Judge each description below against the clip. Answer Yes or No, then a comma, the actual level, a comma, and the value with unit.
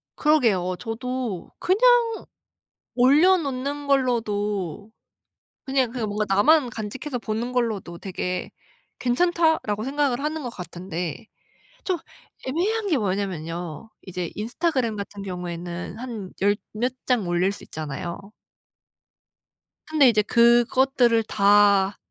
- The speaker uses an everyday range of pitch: No, wide, 5.8 semitones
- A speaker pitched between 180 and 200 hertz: No, high, 225 Hz